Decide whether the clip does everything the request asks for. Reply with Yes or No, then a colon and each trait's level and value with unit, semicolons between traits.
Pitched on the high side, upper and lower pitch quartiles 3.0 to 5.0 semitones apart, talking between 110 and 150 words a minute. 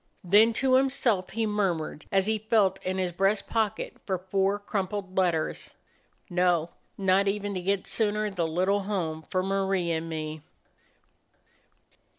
No: high, 195 Hz; narrow, 2.5 semitones; average, 145 wpm